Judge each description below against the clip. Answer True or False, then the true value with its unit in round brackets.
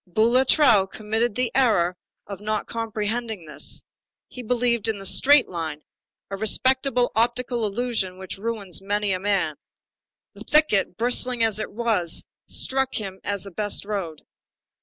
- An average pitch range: True (3.7 semitones)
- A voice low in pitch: False (215 Hz)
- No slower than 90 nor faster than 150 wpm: True (140 wpm)